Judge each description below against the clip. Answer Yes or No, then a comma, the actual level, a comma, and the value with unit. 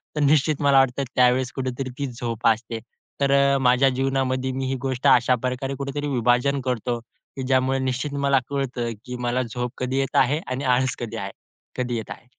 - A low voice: Yes, low, 130 Hz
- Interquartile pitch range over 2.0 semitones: No, narrow, 1.7 semitones